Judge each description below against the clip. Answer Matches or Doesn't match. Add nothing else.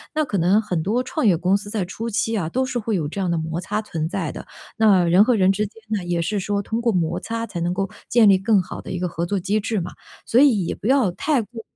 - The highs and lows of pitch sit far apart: Doesn't match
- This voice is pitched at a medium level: Doesn't match